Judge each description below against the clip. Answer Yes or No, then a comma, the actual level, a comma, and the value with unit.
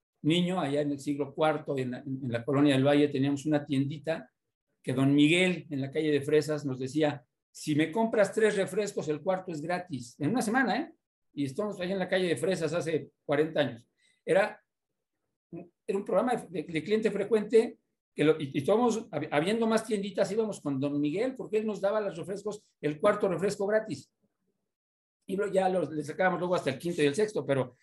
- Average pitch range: No, wide, 5.7 semitones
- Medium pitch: Yes, medium, 165 Hz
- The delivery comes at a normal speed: No, fast, 200 wpm